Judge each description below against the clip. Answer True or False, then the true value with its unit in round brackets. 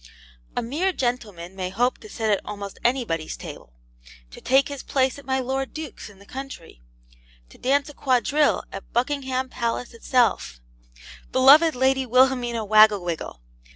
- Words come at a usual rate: True (150 wpm)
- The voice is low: False (250 Hz)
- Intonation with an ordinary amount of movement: True (4.2 semitones)